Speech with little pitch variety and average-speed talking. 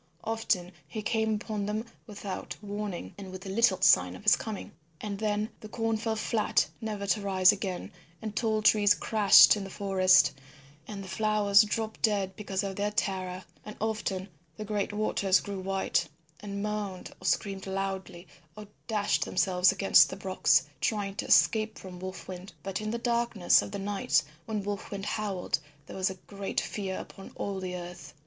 Yes: narrow, 2.0 semitones; average, 175 wpm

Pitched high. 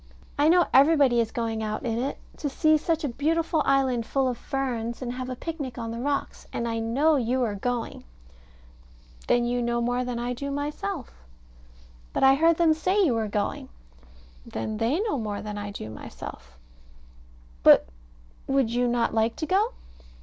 Yes: very high, 250 Hz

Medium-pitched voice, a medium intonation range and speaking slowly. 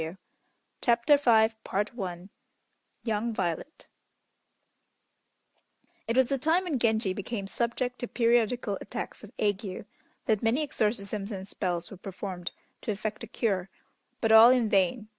No: high, 220 Hz; average, 3.5 semitones; slow, 130 wpm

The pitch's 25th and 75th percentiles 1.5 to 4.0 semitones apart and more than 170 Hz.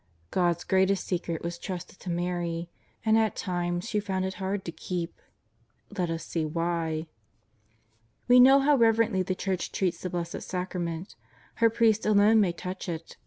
Yes: average, 3.0 semitones; medium, 185 Hz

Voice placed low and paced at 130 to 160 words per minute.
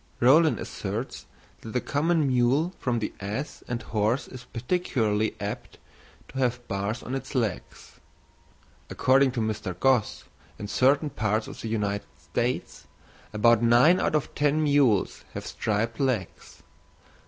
Yes: low, 120 Hz; average, 140 wpm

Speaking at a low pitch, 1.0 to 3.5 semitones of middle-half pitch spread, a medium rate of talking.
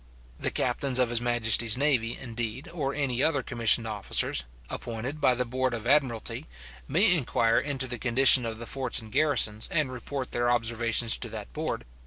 Yes: low, 120 Hz; average, 2.7 semitones; average, 175 wpm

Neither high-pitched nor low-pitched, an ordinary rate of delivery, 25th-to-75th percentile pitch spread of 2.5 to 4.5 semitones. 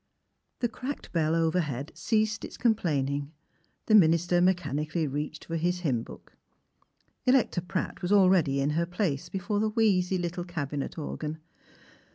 Yes: medium, 175 Hz; average, 145 wpm; average, 4.1 semitones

